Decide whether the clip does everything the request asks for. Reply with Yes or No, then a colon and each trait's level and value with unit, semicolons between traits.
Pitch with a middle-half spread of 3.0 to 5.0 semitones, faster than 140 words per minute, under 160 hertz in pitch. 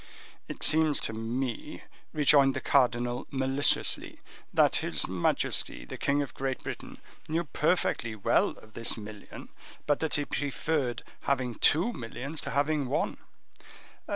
No: average, 3.5 semitones; slow, 135 wpm; low, 135 Hz